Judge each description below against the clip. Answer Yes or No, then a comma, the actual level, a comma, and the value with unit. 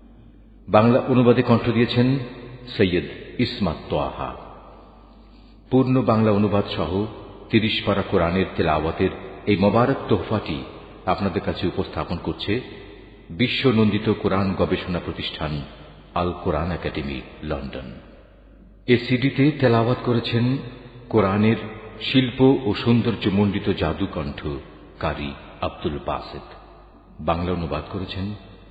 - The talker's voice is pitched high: No, low, 100 Hz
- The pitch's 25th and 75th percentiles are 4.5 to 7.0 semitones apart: Yes, average, 5.1 semitones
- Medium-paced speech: No, slow, 100 wpm